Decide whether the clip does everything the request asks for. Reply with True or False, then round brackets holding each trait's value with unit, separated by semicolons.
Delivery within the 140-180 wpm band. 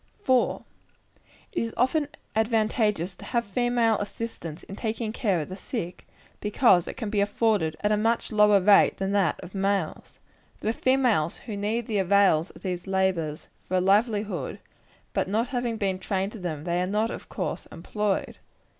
True (175 wpm)